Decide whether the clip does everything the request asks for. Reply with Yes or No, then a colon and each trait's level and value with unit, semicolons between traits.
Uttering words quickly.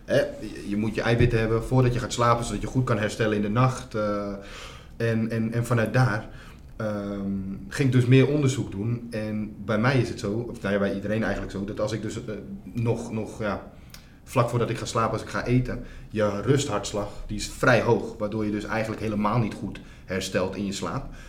Yes: fast, 215 wpm